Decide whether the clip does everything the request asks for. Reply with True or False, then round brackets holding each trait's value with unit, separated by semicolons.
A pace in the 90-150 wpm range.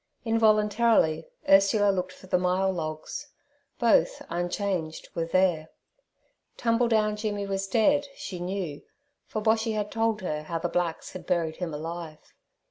True (135 wpm)